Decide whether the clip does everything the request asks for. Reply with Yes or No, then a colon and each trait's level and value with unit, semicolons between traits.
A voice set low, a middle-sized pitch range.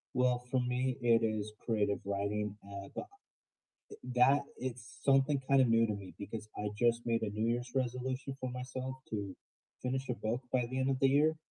Yes: low, 125 Hz; average, 3.3 semitones